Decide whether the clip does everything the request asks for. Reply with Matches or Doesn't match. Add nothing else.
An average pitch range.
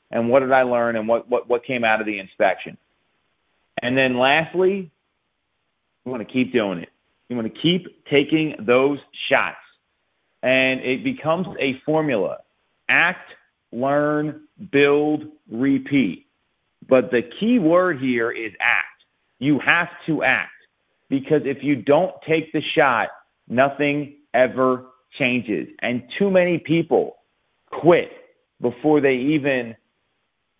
Matches